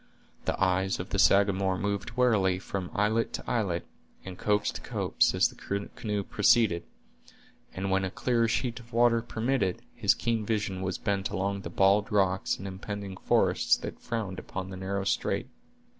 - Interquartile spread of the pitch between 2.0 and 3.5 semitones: Yes, average, 2.8 semitones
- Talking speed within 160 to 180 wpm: Yes, average, 170 wpm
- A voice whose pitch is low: Yes, low, 100 Hz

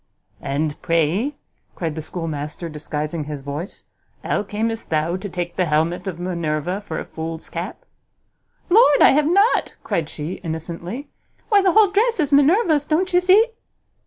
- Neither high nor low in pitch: Yes, medium, 180 Hz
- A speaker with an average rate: Yes, average, 160 wpm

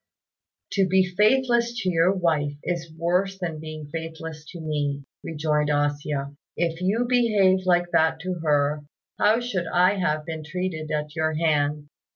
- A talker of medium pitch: Yes, medium, 165 Hz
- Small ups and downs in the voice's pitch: No, average, 3.5 semitones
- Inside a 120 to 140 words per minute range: No, average, 160 wpm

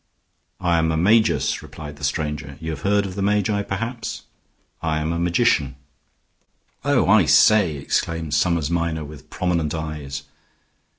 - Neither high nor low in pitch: No, very low, 85 Hz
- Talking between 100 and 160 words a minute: Yes, average, 150 wpm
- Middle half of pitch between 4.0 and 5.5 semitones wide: Yes, average, 4.5 semitones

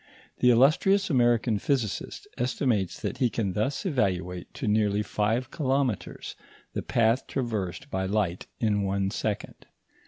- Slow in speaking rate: Yes, slow, 130 wpm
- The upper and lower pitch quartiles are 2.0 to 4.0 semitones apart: No, average, 4.5 semitones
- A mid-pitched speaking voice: No, low, 110 Hz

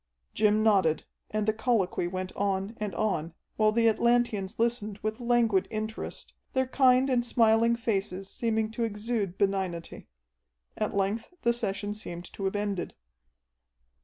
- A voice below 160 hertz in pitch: No, high, 215 Hz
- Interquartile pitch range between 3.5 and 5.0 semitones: No, average, 3.0 semitones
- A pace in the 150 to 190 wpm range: No, average, 140 wpm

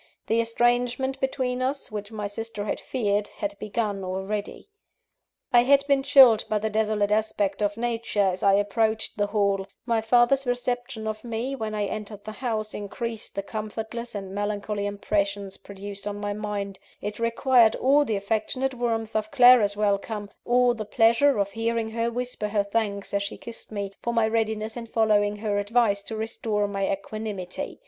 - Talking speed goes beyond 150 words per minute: Yes, average, 170 wpm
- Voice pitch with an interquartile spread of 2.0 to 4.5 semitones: Yes, narrow, 2.4 semitones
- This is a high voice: Yes, high, 215 Hz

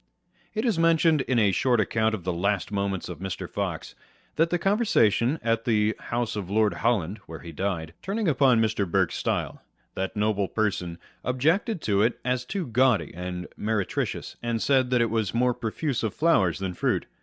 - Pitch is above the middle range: No, low, 110 Hz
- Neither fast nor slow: Yes, average, 190 wpm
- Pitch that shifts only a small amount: No, average, 4.8 semitones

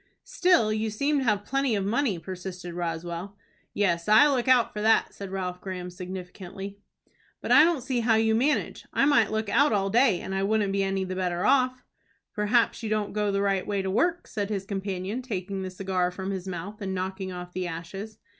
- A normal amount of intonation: Yes, average, 3.1 semitones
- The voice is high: Yes, high, 200 Hz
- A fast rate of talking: Yes, fast, 210 wpm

